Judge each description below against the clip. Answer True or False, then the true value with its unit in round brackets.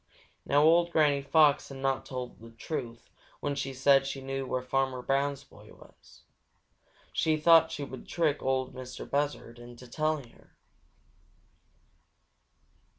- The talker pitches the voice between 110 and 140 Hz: True (135 Hz)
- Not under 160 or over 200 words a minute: False (140 wpm)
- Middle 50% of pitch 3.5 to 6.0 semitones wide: False (2.4 semitones)